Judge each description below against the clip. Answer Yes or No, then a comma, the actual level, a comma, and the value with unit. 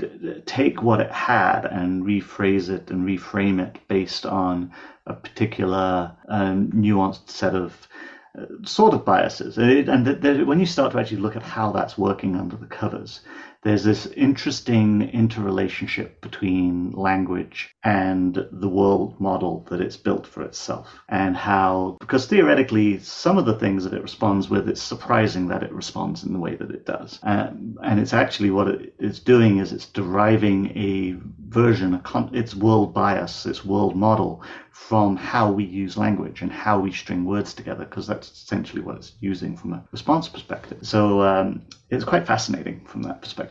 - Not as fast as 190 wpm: Yes, average, 175 wpm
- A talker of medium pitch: No, low, 100 Hz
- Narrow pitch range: Yes, narrow, 2.2 semitones